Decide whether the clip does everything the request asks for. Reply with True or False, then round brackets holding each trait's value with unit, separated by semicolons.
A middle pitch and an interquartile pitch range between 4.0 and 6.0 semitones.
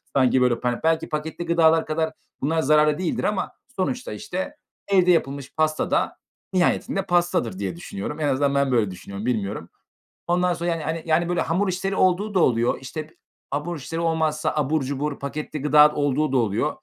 True (155 Hz; 4.3 semitones)